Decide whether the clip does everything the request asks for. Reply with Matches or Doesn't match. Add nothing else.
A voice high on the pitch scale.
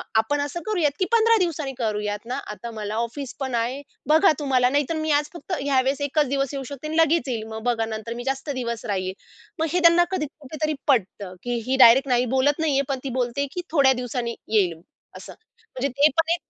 Matches